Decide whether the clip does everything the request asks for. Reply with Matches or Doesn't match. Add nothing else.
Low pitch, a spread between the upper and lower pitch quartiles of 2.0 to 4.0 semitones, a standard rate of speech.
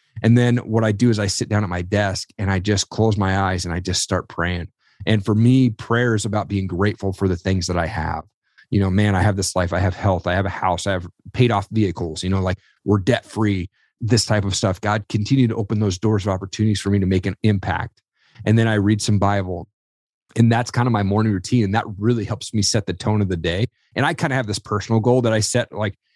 Doesn't match